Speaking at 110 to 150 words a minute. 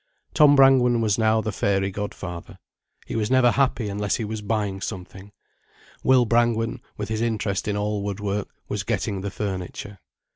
No: average, 170 wpm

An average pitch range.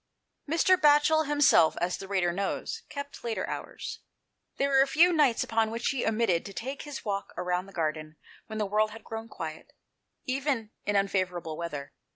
No: wide, 7.4 semitones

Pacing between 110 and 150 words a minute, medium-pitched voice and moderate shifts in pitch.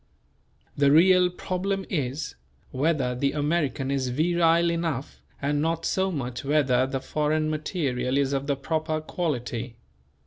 Yes: slow, 135 wpm; medium, 150 Hz; average, 3.8 semitones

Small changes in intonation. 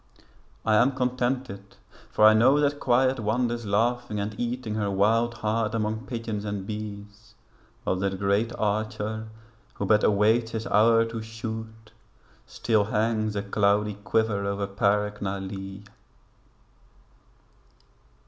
Yes: narrow, 2.1 semitones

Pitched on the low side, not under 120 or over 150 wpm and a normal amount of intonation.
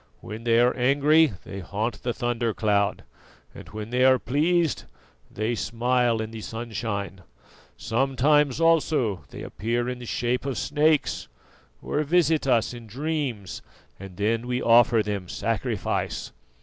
Yes: low, 120 Hz; average, 140 wpm; average, 3.8 semitones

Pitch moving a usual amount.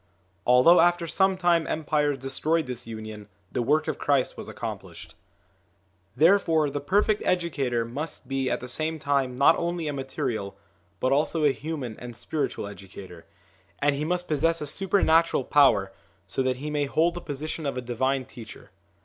Yes: average, 4.4 semitones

